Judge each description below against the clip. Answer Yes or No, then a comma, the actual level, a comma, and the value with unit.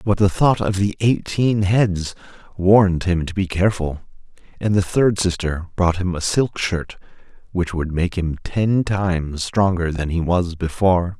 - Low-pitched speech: Yes, very low, 90 Hz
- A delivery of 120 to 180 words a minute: Yes, average, 170 wpm